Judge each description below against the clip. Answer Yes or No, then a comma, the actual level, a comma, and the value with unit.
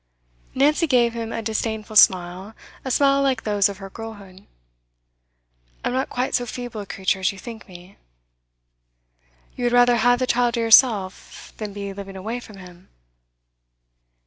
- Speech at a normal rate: Yes, average, 160 wpm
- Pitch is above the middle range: Yes, high, 220 Hz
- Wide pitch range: No, average, 3.9 semitones